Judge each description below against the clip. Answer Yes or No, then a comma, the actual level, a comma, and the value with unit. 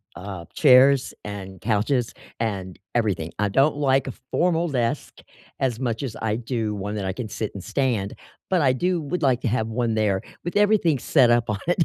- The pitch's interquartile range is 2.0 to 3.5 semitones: No, average, 4.8 semitones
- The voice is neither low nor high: No, low, 120 Hz